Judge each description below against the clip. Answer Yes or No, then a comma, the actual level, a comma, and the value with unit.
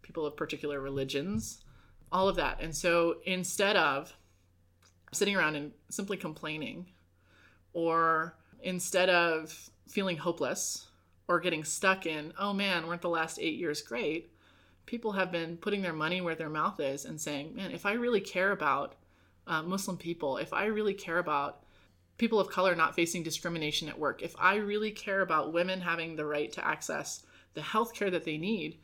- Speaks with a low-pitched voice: No, medium, 165 Hz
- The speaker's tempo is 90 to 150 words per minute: No, average, 175 wpm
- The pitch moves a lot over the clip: No, average, 4.0 semitones